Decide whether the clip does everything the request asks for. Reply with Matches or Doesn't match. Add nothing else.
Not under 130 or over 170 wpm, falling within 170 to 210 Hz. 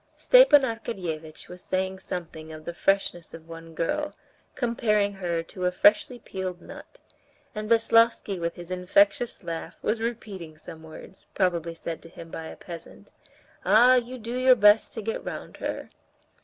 Matches